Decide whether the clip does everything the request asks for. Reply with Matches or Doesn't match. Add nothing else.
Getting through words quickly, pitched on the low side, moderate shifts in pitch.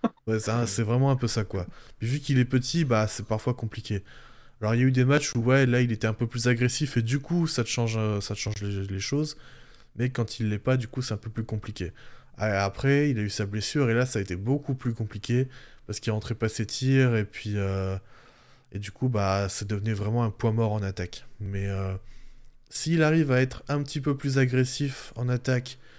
Matches